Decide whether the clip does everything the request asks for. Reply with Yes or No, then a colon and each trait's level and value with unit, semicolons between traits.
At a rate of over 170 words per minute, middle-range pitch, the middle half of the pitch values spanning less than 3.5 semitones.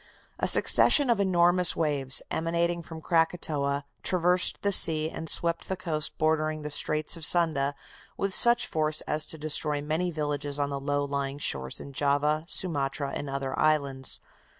No: average, 160 wpm; medium, 155 Hz; average, 2.9 semitones